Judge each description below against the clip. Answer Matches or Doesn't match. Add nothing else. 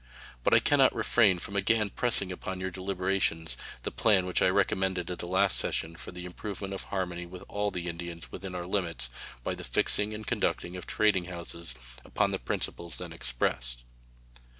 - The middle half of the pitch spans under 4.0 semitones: Matches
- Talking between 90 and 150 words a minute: Doesn't match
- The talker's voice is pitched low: Matches